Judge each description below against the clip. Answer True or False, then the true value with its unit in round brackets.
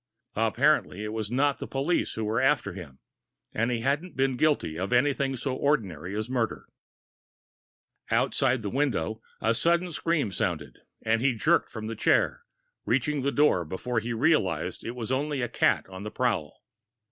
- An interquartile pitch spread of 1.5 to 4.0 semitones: False (4.7 semitones)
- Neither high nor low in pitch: False (120 Hz)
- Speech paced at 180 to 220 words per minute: False (170 wpm)